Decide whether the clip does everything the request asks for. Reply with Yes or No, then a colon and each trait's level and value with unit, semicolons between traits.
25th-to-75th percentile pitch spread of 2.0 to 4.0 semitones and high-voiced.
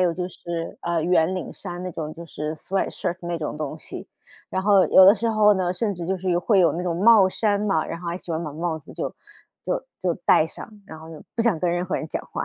No: narrow, 2.5 semitones; medium, 175 Hz